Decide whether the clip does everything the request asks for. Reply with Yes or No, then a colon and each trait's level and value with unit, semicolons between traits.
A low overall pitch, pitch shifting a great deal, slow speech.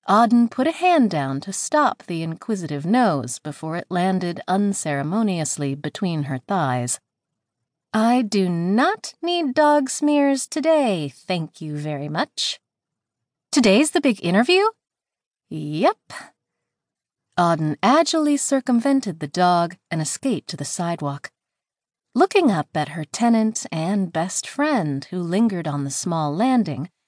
No: medium, 185 Hz; wide, 8.9 semitones; slow, 125 wpm